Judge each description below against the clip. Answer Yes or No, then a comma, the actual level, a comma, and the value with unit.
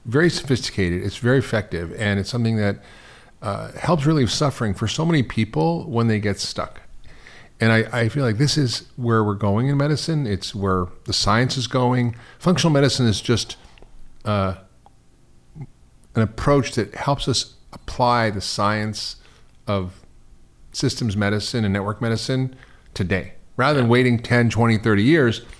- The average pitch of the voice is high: No, low, 115 Hz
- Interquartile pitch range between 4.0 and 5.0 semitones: Yes, average, 4.4 semitones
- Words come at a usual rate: Yes, average, 155 wpm